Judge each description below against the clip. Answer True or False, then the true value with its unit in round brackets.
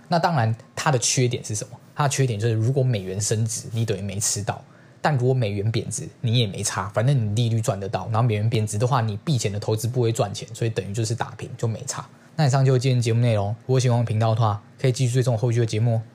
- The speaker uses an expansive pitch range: False (2.7 semitones)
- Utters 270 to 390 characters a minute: False (400 characters per minute)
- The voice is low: True (120 Hz)